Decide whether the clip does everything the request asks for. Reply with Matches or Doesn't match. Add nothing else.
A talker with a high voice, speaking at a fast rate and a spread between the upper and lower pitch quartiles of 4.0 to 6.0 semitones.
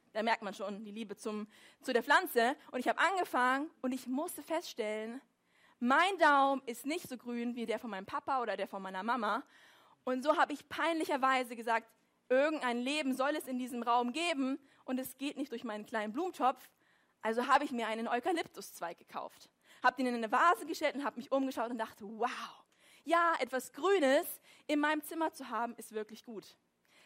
Matches